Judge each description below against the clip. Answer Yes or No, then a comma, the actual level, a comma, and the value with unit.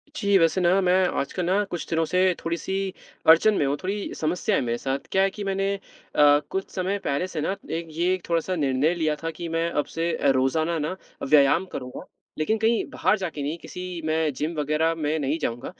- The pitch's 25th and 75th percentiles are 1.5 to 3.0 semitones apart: No, average, 3.6 semitones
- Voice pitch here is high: No, medium, 165 Hz